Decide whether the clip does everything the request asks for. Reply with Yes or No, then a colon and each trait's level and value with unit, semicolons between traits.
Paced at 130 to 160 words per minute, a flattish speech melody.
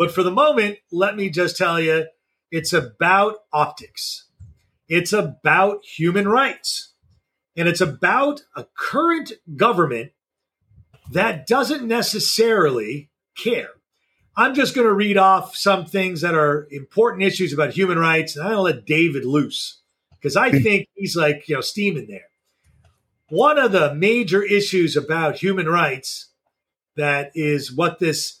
No: average, 140 wpm; average, 4.5 semitones